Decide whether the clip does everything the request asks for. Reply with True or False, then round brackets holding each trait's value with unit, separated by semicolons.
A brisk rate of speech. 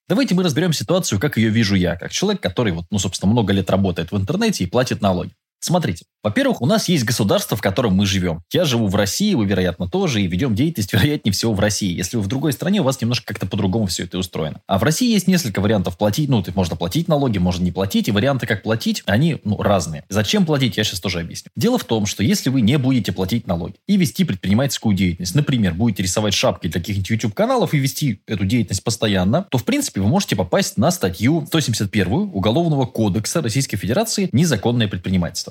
True (220 wpm)